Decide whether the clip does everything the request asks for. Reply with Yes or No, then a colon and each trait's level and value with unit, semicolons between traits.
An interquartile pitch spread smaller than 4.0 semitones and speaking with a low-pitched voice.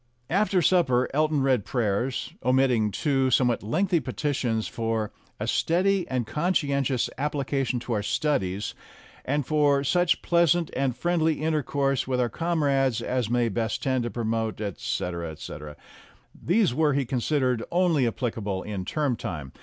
No: average, 4.8 semitones; low, 130 Hz